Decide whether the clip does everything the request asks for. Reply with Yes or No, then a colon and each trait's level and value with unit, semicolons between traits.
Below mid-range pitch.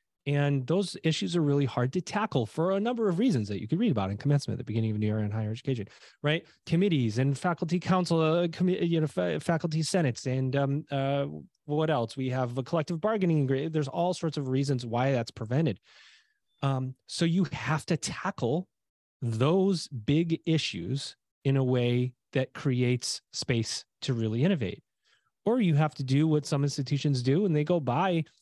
No: medium, 145 Hz